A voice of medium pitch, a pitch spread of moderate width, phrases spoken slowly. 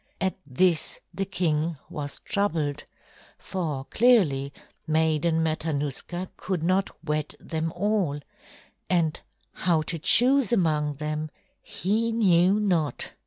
Yes: medium, 165 Hz; average, 3.9 semitones; slow, 110 wpm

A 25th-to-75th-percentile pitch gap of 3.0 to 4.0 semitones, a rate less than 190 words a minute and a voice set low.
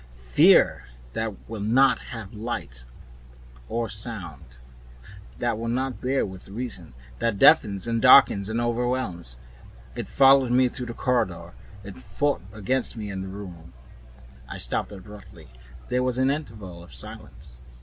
No: average, 4.9 semitones; average, 145 wpm; low, 110 Hz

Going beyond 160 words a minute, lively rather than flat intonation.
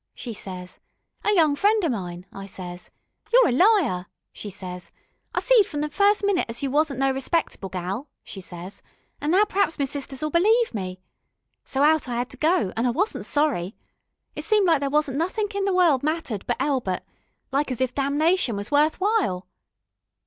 Yes: average, 190 wpm; wide, 8.9 semitones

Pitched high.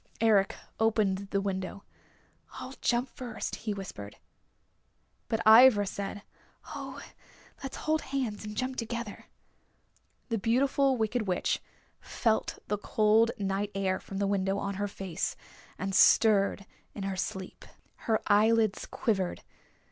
Yes: high, 210 Hz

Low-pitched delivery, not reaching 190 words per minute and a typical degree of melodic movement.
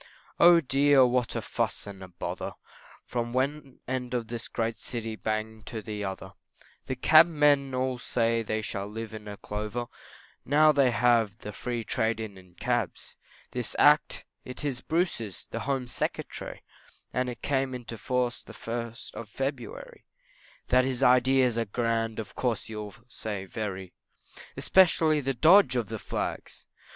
Yes: low, 120 Hz; average, 155 wpm; average, 3.1 semitones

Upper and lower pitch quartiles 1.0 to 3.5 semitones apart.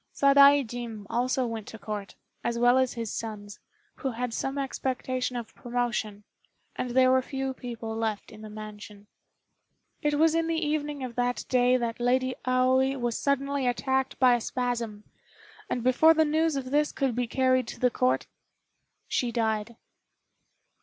Yes: narrow, 2.6 semitones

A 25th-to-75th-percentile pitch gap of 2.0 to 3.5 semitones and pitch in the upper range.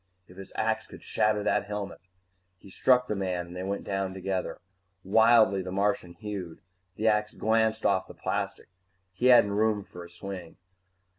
No: narrow, 2.5 semitones; low, 100 Hz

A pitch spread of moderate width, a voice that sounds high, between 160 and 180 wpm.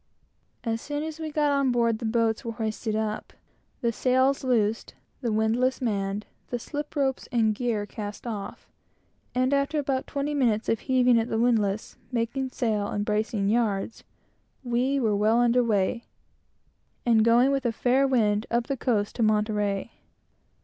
Yes: average, 3.2 semitones; high, 235 Hz; average, 165 wpm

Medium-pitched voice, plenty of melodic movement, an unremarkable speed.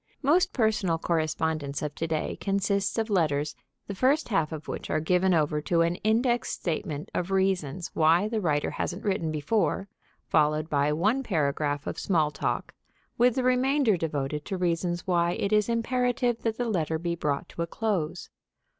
Yes: medium, 175 Hz; wide, 5.8 semitones; average, 170 wpm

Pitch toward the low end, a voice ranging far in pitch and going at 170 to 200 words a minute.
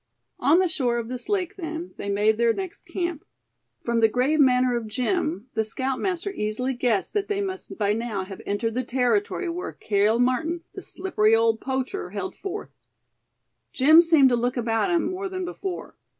No: very high, 255 Hz; wide, 7.5 semitones; average, 180 wpm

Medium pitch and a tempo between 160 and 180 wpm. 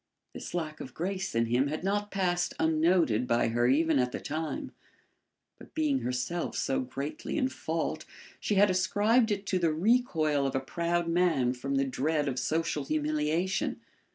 Yes: medium, 160 Hz; average, 170 wpm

